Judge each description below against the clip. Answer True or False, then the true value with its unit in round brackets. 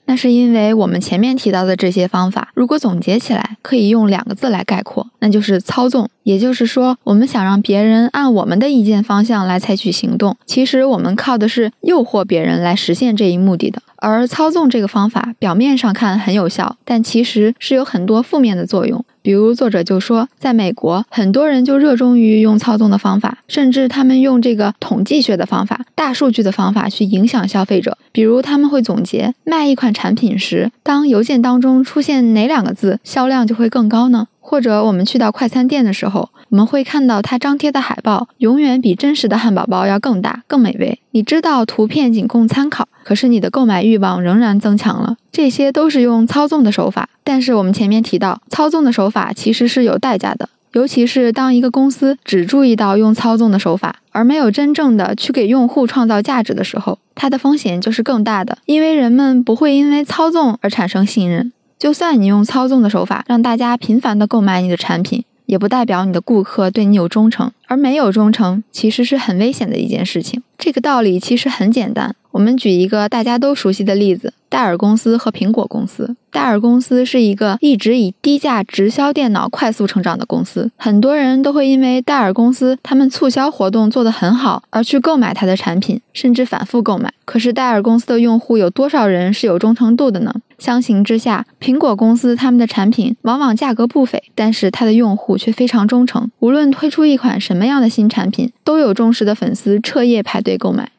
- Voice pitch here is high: True (230 Hz)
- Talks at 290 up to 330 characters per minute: True (325 characters per minute)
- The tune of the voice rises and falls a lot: False (3.6 semitones)